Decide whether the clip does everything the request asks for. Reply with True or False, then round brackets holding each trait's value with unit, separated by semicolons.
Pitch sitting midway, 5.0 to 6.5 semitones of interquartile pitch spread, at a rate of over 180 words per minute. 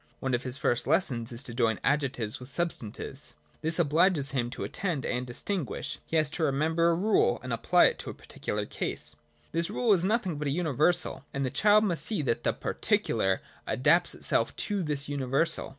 True (150 Hz; 5.3 semitones; 200 wpm)